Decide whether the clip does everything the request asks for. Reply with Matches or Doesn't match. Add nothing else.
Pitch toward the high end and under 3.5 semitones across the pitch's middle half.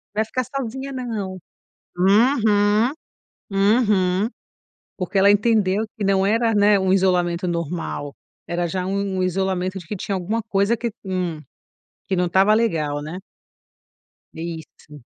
Matches